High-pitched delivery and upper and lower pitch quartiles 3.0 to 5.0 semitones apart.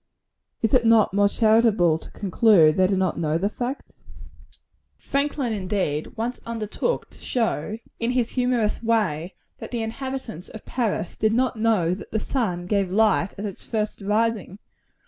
Yes: high, 215 Hz; average, 3.6 semitones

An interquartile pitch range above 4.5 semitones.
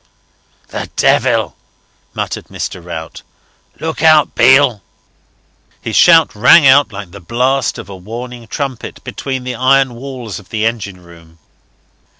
Yes: average, 5.1 semitones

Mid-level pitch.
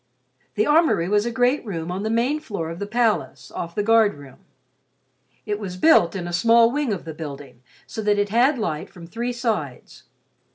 No: high, 210 Hz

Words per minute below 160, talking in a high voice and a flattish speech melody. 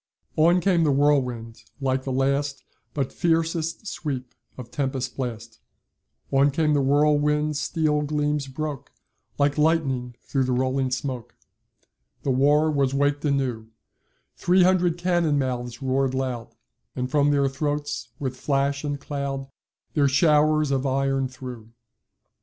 No: slow, 135 wpm; medium, 140 Hz; narrow, 2.3 semitones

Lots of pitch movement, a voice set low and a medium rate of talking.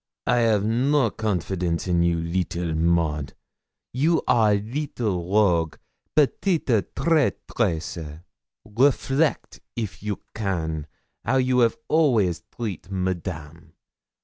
No: wide, 6.4 semitones; low, 100 Hz; slow, 100 wpm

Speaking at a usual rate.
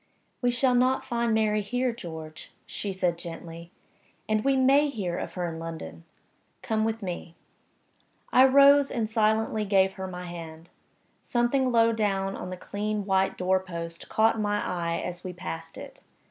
Yes: average, 165 wpm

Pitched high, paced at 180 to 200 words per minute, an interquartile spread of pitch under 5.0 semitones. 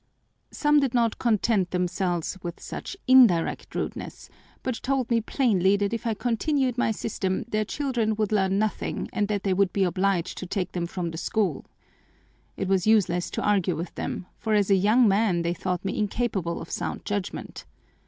Yes: high, 205 Hz; average, 185 wpm; average, 3.8 semitones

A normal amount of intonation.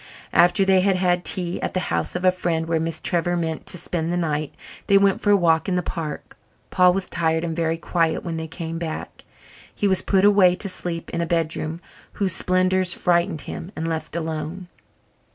No: narrow, 2.1 semitones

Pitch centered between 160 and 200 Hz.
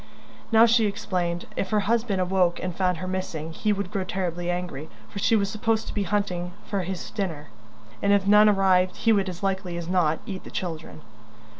Yes: high, 190 Hz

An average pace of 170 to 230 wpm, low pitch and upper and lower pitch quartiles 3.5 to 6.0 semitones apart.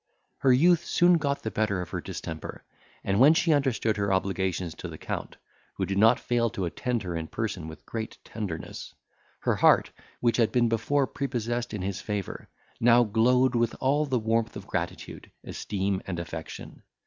Yes: average, 180 wpm; low, 115 Hz; average, 4.4 semitones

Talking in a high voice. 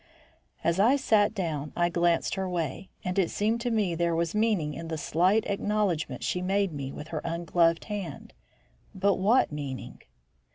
No: medium, 180 Hz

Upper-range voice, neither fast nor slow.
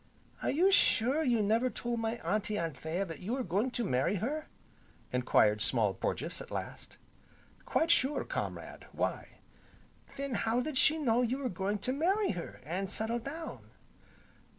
Yes: high, 225 Hz; average, 165 wpm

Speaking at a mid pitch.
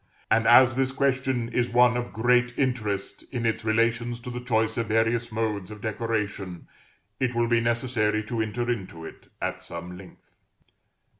No: low, 115 Hz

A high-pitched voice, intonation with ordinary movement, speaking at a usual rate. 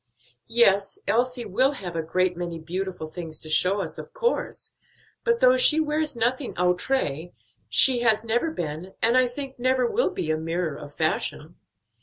No: high, 200 Hz; wide, 7.3 semitones; average, 170 wpm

